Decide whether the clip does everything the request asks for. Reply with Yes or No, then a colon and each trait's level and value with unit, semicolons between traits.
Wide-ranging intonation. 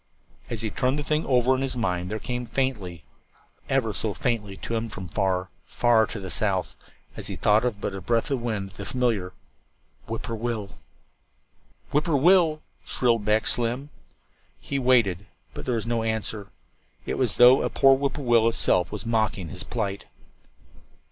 No: average, 3.9 semitones